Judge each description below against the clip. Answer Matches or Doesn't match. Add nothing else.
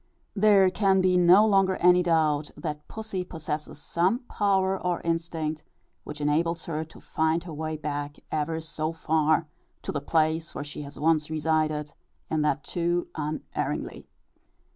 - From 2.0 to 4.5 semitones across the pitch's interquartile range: Matches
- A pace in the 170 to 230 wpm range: Doesn't match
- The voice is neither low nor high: Matches